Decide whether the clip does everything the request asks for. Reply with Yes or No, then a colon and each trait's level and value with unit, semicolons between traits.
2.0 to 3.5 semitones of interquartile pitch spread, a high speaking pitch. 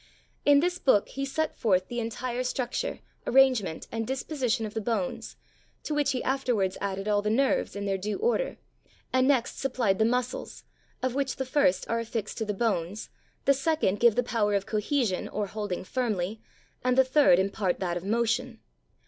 No: average, 4.4 semitones; high, 235 Hz